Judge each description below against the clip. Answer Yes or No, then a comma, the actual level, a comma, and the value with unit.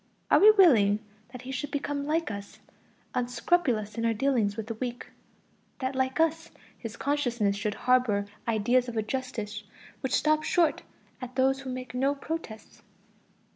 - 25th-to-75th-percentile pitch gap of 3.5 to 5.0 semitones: Yes, average, 4.2 semitones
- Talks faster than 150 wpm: Yes, average, 160 wpm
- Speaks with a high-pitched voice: Yes, very high, 255 Hz